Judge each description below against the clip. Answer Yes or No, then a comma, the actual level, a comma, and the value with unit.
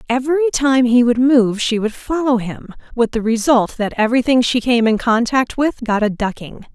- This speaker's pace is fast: No, average, 195 wpm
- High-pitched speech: Yes, high, 240 Hz